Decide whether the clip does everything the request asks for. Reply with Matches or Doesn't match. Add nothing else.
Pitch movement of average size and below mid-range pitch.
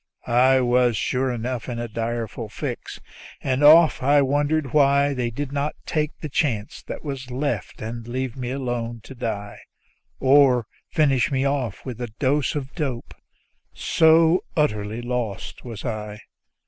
Matches